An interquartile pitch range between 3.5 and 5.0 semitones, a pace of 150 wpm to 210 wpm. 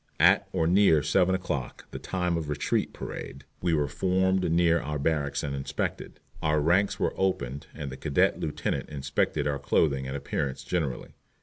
Yes: average, 3.9 semitones; average, 170 wpm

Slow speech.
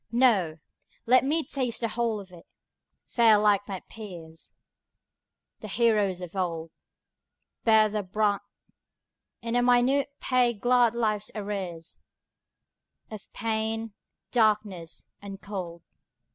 Yes: slow, 115 wpm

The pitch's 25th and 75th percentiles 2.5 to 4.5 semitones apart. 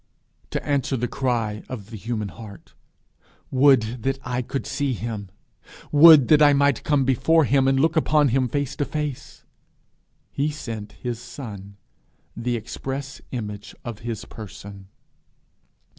Yes: average, 4.2 semitones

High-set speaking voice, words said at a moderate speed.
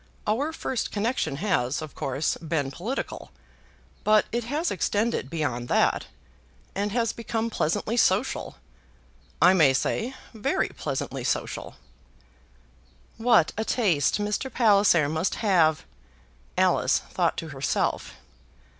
No: high, 205 Hz; slow, 115 wpm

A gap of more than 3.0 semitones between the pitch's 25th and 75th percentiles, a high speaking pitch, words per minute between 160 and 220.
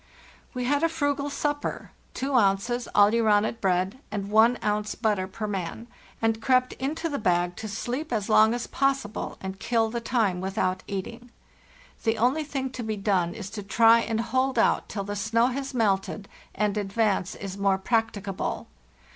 Yes: average, 3.7 semitones; high, 220 Hz; average, 165 wpm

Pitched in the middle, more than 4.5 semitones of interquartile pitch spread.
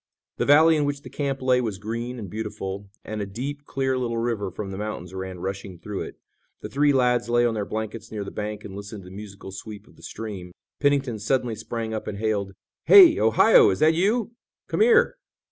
No: low, 110 Hz; average, 5.1 semitones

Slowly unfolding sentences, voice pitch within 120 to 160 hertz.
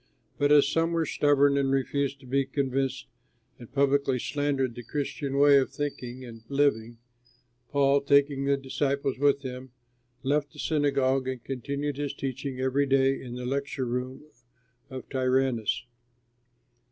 No: average, 145 wpm; low, 135 Hz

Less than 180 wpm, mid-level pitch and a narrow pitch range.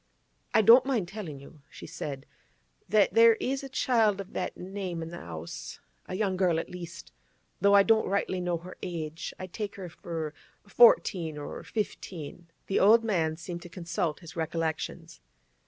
No: average, 170 wpm; medium, 180 Hz; average, 4.0 semitones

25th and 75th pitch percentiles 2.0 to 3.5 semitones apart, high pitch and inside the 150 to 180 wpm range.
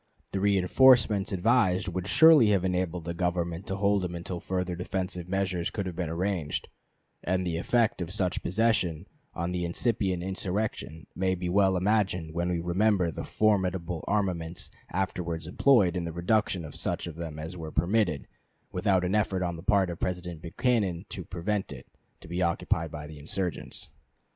No: narrow, 2.4 semitones; very low, 90 Hz; average, 170 wpm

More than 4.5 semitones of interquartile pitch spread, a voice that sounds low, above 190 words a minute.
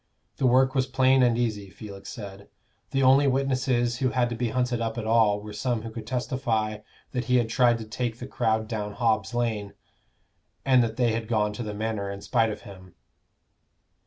No: average, 2.8 semitones; low, 115 Hz; average, 200 wpm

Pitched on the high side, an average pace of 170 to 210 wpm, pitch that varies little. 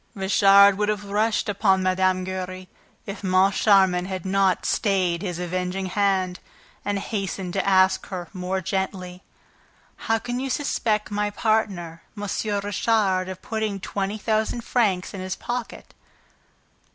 No: high, 195 Hz; slow, 135 wpm; narrow, 2.0 semitones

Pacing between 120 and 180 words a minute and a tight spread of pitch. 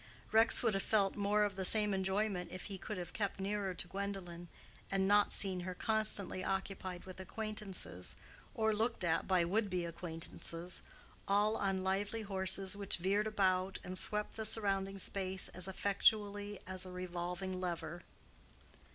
Yes: average, 160 wpm; narrow, 2.0 semitones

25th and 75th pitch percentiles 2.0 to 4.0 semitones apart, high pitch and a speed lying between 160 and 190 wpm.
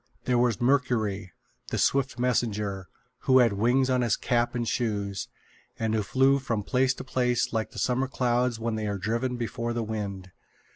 No: average, 2.9 semitones; low, 120 Hz; average, 180 wpm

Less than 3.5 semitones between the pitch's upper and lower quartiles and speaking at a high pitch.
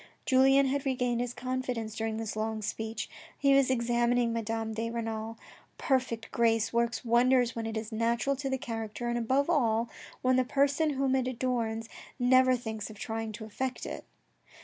Yes: narrow, 2.5 semitones; high, 235 Hz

